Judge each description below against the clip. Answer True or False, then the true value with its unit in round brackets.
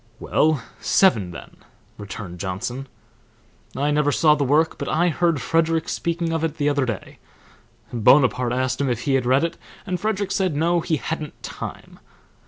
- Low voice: False (145 Hz)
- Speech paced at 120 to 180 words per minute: True (170 wpm)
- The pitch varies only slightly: False (4.6 semitones)